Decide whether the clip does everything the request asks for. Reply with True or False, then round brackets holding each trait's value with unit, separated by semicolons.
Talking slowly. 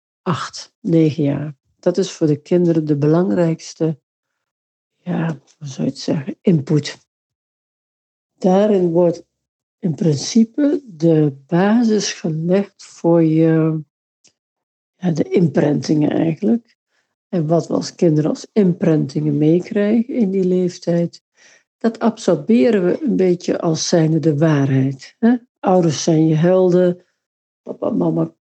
True (115 wpm)